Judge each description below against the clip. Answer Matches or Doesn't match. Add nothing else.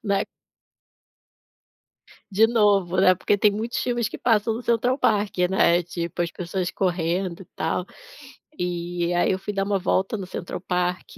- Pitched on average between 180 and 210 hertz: Matches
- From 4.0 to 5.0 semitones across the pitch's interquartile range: Doesn't match